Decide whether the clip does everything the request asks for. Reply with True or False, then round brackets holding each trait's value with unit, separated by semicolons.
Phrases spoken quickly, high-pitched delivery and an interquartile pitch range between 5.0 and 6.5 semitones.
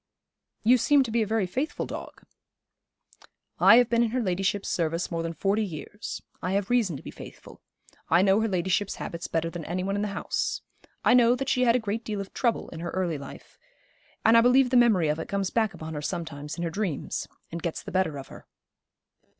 True (225 wpm; 195 Hz; 5.5 semitones)